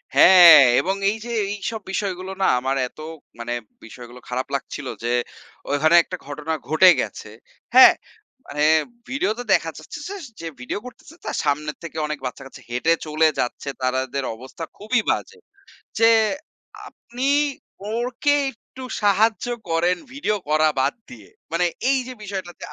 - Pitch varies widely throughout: Yes, wide, 7.0 semitones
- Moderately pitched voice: Yes, medium, 165 Hz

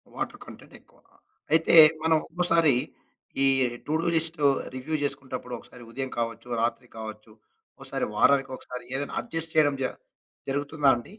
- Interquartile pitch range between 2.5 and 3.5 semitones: No, average, 4.6 semitones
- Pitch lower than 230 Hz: Yes, medium, 140 Hz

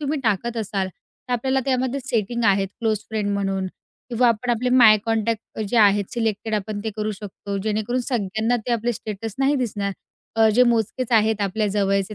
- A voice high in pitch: Yes, high, 220 Hz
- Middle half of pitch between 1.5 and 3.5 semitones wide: Yes, average, 2.8 semitones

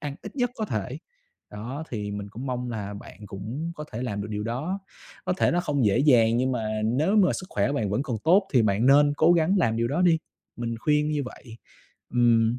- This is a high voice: No, low, 125 Hz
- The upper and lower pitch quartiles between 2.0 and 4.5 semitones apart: No, wide, 5.4 semitones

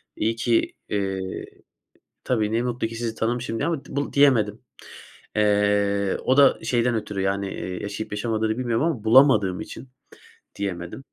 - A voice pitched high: No, low, 110 Hz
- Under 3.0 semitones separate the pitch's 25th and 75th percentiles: No, average, 3.3 semitones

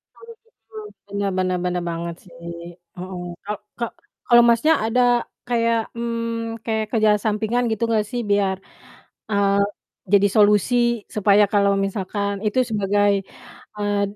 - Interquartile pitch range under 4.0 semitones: Yes, narrow, 2.5 semitones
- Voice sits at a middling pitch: No, high, 210 Hz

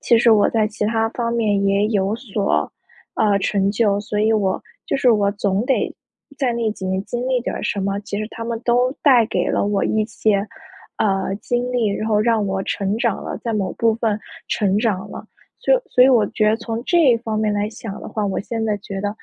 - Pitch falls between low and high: No, high, 215 Hz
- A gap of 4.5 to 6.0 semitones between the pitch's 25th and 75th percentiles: No, narrow, 2.4 semitones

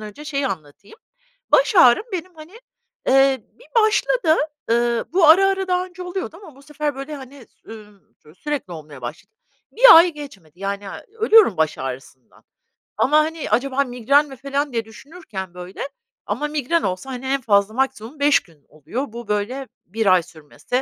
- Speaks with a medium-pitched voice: No, very high, 270 Hz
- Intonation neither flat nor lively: No, wide, 7.5 semitones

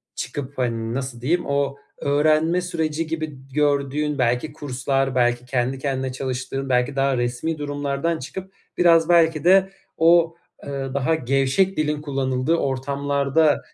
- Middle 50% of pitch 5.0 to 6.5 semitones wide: No, average, 3.3 semitones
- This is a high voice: No, medium, 140 Hz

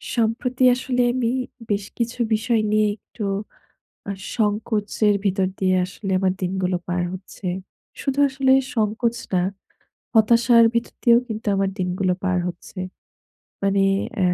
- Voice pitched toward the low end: No, high, 215 Hz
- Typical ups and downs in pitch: Yes, average, 3.6 semitones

